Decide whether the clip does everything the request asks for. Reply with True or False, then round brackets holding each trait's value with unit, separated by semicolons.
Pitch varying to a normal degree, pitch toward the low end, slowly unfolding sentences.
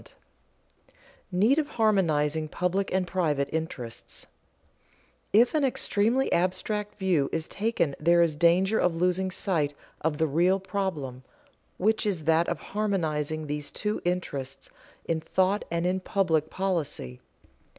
False (4.0 semitones; 180 Hz; 130 wpm)